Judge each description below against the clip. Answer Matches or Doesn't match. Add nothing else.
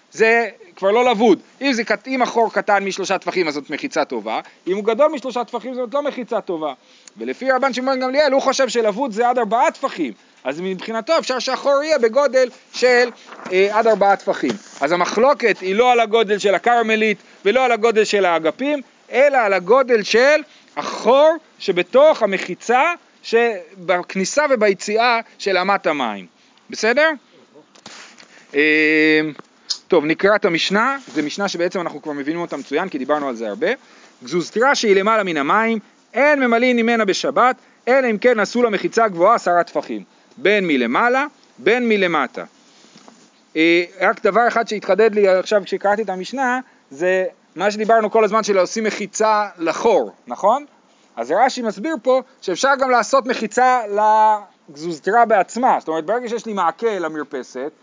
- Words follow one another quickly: Matches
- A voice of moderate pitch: Doesn't match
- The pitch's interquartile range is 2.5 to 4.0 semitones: Doesn't match